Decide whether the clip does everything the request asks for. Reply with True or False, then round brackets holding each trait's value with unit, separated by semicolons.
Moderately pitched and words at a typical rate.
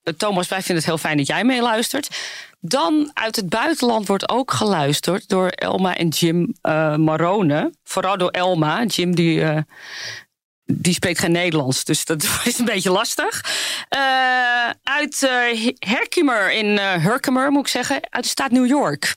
False (195 Hz; 165 wpm)